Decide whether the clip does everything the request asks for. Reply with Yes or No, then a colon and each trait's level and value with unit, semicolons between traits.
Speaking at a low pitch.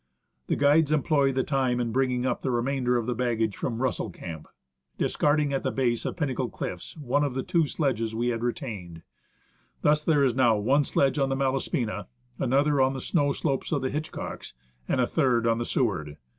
Yes: low, 130 Hz